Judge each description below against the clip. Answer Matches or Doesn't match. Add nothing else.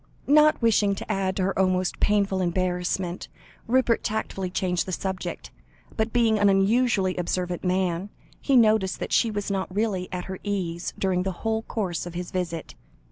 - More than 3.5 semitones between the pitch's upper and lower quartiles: Doesn't match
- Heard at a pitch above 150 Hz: Matches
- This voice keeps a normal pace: Matches